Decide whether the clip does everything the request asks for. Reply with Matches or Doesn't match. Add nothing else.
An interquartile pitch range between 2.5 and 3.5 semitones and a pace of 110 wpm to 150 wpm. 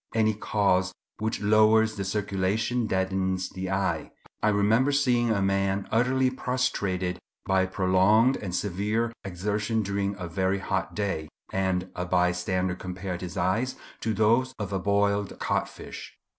Matches